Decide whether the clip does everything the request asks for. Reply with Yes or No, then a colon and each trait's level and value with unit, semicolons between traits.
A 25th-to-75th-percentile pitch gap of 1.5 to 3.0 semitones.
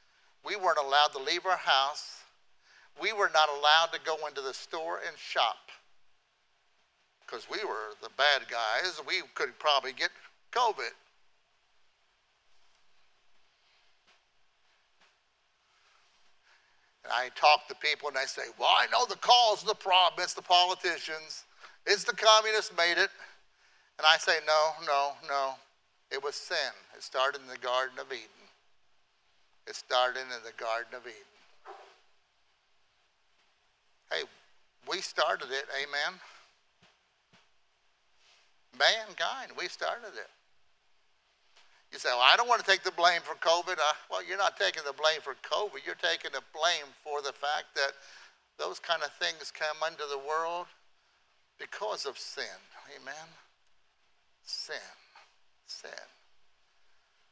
No: average, 4.2 semitones